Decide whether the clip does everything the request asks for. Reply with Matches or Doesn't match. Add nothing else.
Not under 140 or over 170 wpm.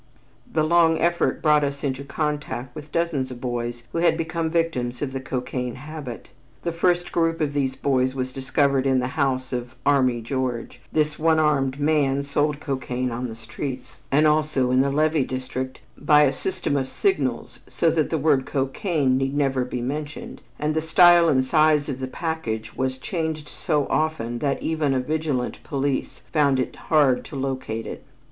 Doesn't match